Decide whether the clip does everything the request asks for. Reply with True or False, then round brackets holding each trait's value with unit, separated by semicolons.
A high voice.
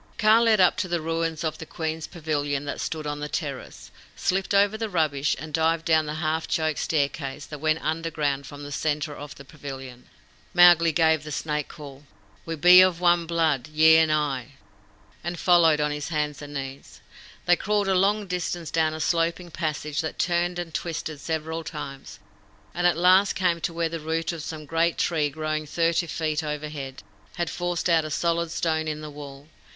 False (160 Hz)